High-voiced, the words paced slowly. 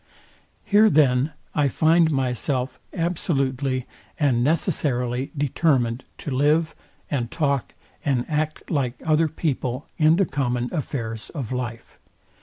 No: medium, 140 Hz; slow, 115 wpm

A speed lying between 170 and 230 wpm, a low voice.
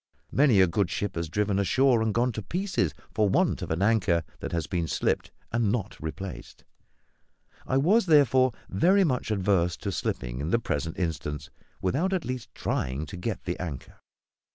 Yes: average, 175 wpm; low, 100 Hz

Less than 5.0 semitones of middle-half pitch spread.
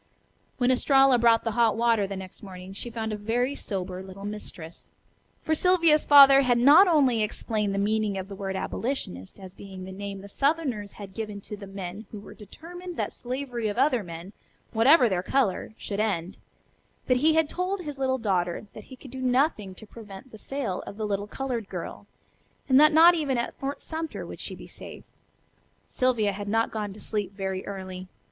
No: average, 5.3 semitones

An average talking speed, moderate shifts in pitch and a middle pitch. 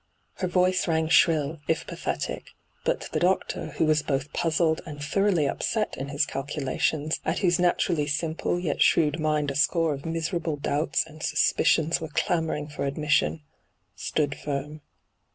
No: average, 155 wpm; narrow, 2.2 semitones; medium, 155 Hz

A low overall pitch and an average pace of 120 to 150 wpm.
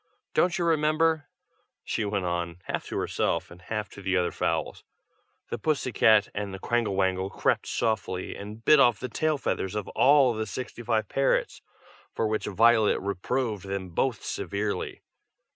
No: low, 110 Hz; average, 165 wpm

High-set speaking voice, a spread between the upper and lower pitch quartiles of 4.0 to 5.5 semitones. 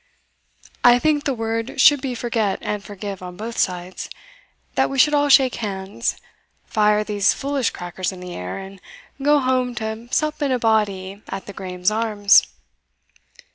Yes: high, 220 Hz; average, 4.7 semitones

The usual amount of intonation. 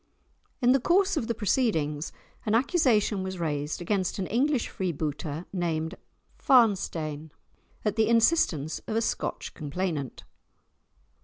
No: wide, 6.8 semitones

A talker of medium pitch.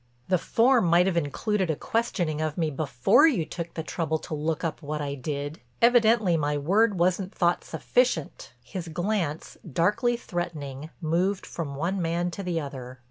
Yes: medium, 170 Hz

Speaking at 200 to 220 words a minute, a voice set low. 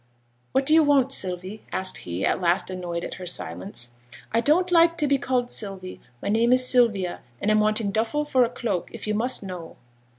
No: fast, 205 wpm; high, 215 Hz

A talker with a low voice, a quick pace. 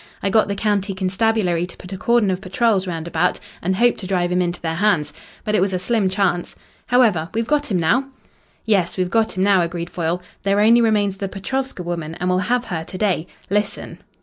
No: high, 190 Hz; fast, 220 wpm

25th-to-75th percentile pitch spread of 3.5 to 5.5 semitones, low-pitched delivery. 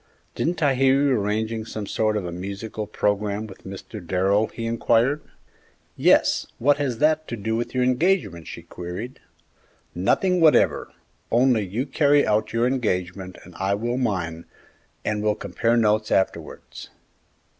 Yes: average, 4.3 semitones; low, 110 Hz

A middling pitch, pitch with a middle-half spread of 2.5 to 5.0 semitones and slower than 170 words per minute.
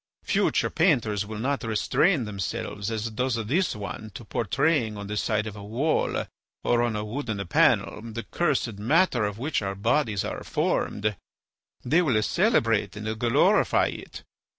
No: low, 110 Hz; average, 3.5 semitones; average, 155 wpm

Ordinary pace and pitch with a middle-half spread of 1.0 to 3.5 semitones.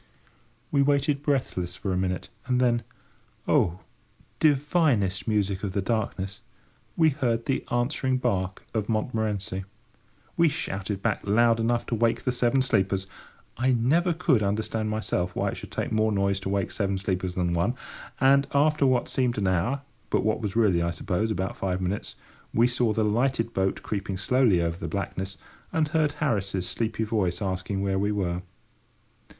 No: average, 160 wpm; average, 4.8 semitones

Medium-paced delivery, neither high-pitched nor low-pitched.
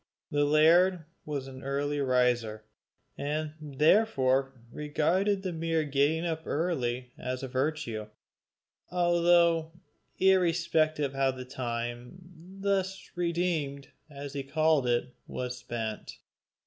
No: slow, 110 wpm; medium, 145 Hz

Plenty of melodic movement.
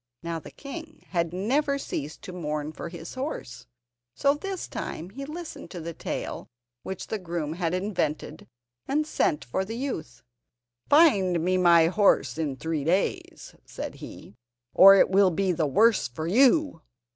Yes: wide, 8.2 semitones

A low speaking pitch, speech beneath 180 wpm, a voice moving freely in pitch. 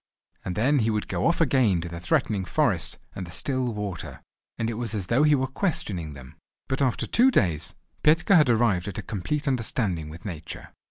No: low, 110 Hz; fast, 205 wpm; wide, 7.0 semitones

